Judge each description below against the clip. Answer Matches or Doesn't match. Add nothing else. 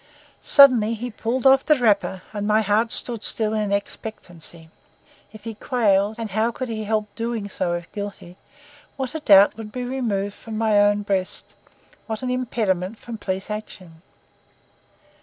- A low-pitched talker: Doesn't match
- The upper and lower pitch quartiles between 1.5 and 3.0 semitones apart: Matches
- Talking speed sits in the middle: Matches